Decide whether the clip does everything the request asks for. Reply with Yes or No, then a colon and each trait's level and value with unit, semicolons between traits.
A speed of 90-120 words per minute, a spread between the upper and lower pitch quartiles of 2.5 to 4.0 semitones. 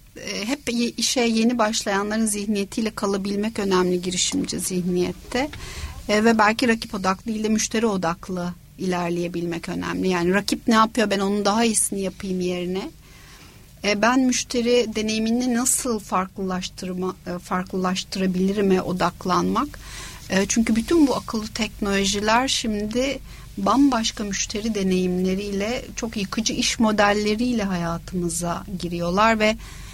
Yes: average, 110 wpm; average, 3.7 semitones